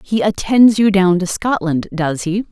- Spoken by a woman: Yes, female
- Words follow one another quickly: No, average, 165 wpm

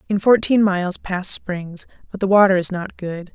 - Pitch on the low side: No, high, 190 Hz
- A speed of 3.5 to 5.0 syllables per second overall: Yes, 4.8 syllables/s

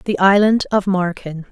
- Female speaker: Yes, female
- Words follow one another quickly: No, average, 160 wpm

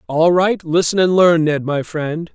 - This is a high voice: No, medium, 165 Hz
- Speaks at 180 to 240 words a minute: Yes, fast, 205 wpm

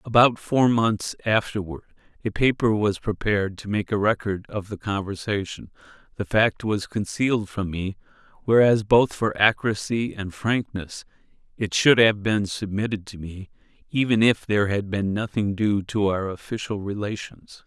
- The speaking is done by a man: Yes, male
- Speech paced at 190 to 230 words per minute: No, average, 155 wpm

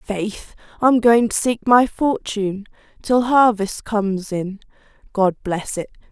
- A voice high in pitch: Yes, high, 215 Hz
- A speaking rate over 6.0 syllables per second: No, 3.9 syllables/s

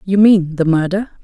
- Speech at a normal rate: Yes, average, 145 wpm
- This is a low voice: No, medium, 185 Hz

